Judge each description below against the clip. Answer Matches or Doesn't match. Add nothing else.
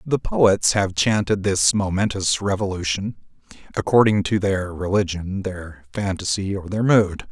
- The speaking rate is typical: Doesn't match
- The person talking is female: Doesn't match